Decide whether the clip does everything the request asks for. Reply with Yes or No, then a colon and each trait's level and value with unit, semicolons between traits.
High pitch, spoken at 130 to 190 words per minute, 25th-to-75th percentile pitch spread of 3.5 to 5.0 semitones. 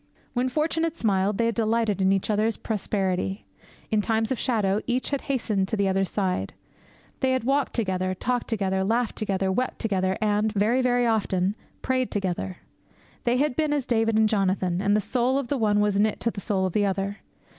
No: high, 215 Hz; average, 200 wpm; average, 3.9 semitones